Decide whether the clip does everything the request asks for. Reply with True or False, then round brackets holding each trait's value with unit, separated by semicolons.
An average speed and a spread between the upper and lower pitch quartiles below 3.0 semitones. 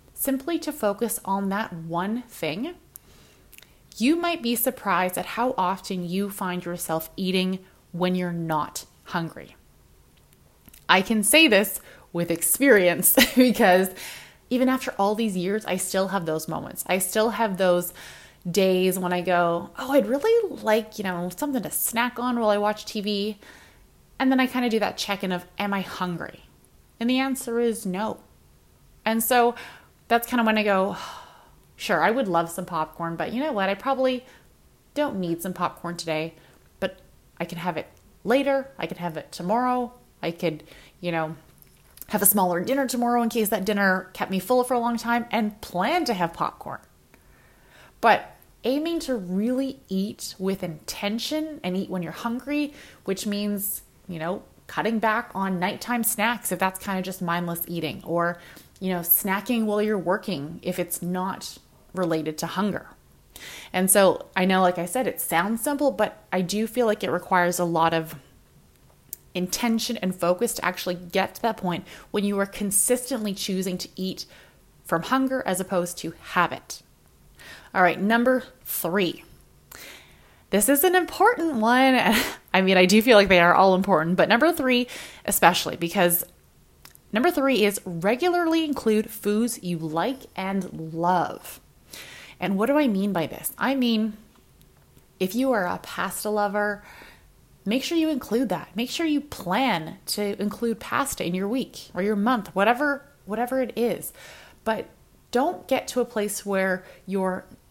False (170 wpm; 4.9 semitones)